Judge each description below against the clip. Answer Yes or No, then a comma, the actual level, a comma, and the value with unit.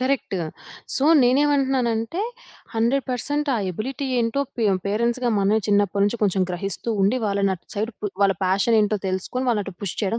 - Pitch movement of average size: Yes, average, 4.2 semitones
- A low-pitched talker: No, high, 225 Hz